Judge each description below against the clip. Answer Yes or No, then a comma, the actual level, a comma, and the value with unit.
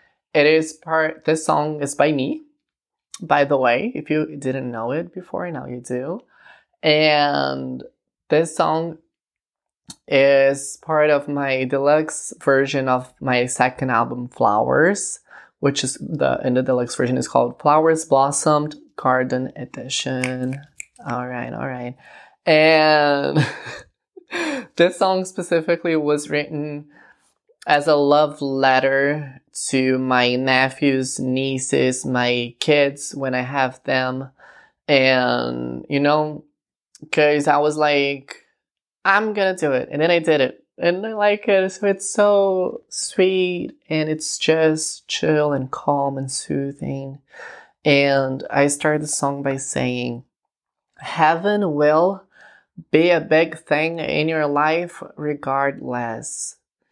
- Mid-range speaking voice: Yes, medium, 145 Hz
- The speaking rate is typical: No, slow, 125 wpm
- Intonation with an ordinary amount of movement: Yes, average, 3.2 semitones